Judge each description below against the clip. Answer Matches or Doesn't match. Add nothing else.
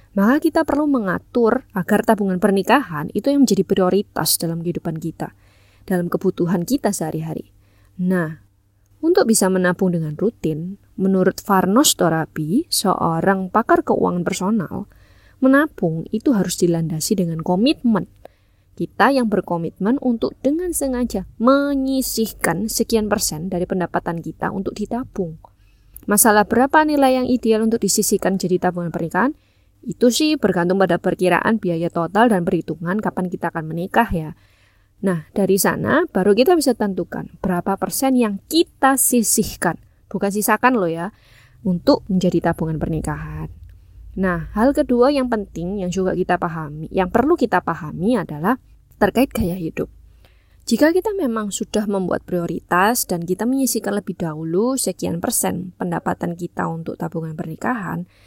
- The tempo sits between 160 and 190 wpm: Doesn't match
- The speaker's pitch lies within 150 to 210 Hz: Matches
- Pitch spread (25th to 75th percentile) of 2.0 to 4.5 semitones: Doesn't match